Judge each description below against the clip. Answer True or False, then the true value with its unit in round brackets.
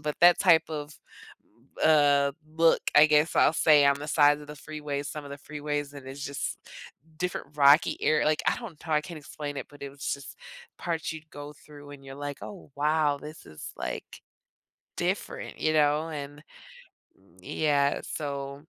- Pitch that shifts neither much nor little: False (1.5 semitones)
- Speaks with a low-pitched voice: False (150 Hz)